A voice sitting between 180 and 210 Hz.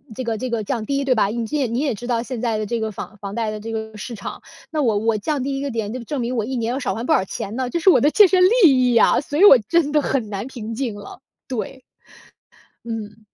No: high, 235 Hz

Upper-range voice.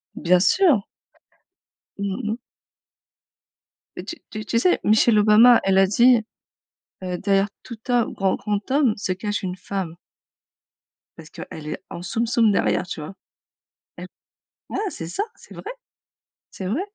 Yes: high, 205 Hz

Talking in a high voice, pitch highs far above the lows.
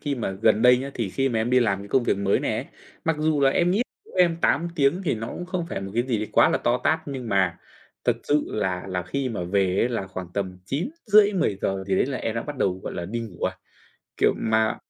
No: low, 115 Hz; wide, 6.8 semitones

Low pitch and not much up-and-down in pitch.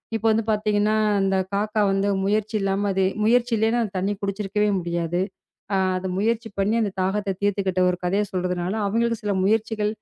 No: high, 205 Hz; narrow, 2.1 semitones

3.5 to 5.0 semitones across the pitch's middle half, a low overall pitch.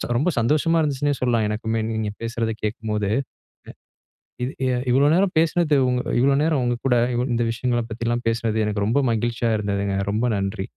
Yes: average, 3.8 semitones; low, 120 Hz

